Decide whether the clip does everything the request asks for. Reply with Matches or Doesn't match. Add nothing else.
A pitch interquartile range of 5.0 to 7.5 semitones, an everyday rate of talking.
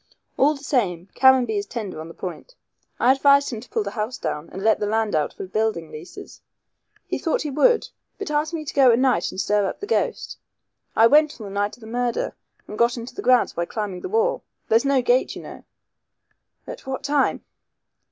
Doesn't match